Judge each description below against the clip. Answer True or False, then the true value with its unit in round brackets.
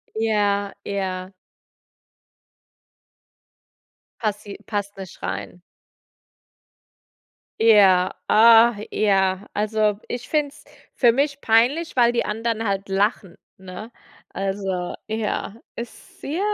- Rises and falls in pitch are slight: False (3.0 semitones)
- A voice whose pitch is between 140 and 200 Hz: False (210 Hz)